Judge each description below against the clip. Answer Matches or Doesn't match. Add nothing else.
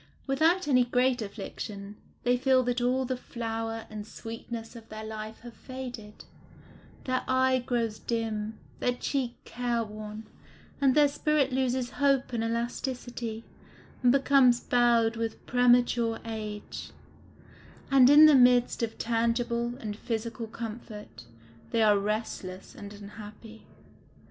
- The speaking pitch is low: Doesn't match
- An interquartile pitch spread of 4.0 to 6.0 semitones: Doesn't match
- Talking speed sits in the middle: Doesn't match